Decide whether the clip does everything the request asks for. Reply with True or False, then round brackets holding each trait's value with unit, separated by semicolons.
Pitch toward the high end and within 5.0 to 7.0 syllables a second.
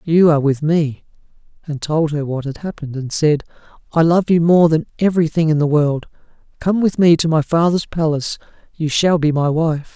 False (155 Hz; 5.4 syllables/s)